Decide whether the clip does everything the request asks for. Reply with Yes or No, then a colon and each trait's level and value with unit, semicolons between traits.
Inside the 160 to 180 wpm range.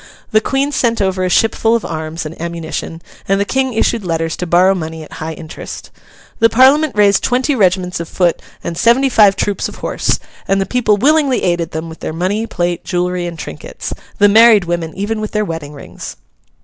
No: average, 200 wpm